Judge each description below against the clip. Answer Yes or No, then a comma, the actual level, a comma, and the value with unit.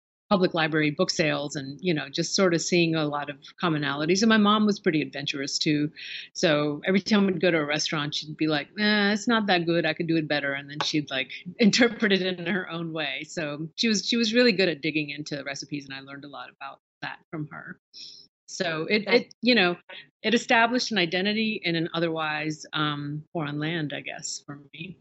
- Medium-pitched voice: Yes, medium, 165 Hz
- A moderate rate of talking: No, fast, 220 wpm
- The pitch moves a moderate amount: Yes, average, 4.3 semitones